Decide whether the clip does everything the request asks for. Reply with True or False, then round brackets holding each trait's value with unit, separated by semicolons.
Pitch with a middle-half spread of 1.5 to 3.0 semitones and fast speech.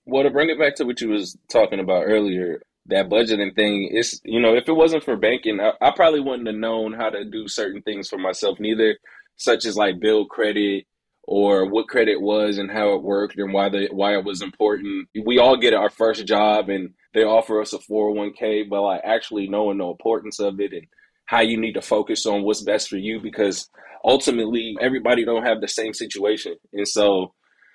True (2.6 semitones; 215 wpm)